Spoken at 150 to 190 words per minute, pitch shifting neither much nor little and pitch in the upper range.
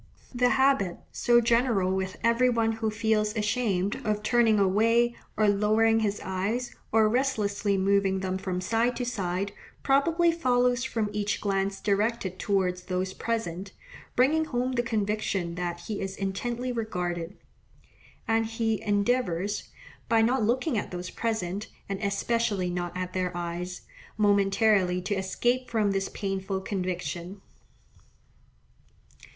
No: slow, 135 wpm; average, 3.6 semitones; high, 210 Hz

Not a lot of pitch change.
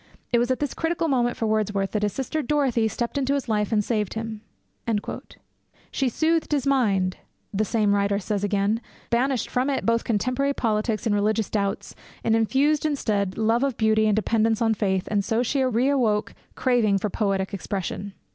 No: average, 3.8 semitones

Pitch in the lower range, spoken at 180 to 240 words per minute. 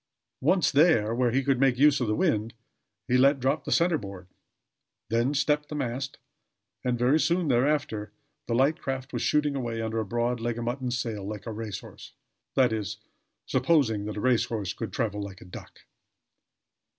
Yes: low, 125 Hz; average, 185 wpm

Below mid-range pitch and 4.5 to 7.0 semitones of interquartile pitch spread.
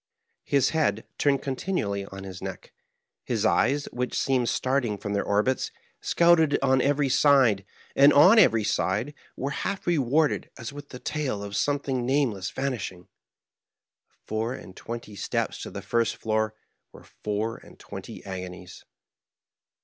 Yes: low, 125 Hz; average, 5.3 semitones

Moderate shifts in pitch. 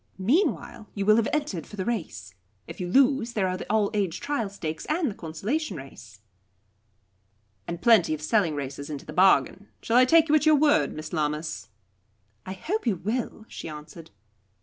No: wide, 7.5 semitones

